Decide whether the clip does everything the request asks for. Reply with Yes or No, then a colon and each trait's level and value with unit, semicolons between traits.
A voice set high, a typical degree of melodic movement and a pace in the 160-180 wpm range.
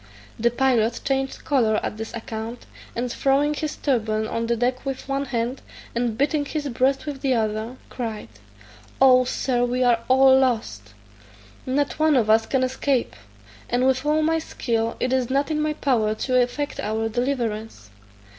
Yes: very high, 250 Hz; average, 3.1 semitones; average, 170 wpm